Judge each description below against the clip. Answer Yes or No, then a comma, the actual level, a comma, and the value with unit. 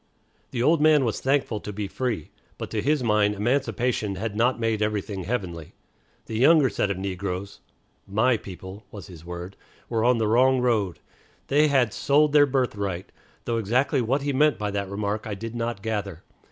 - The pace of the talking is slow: No, average, 180 wpm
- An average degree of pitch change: Yes, average, 4.2 semitones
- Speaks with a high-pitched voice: No, low, 110 Hz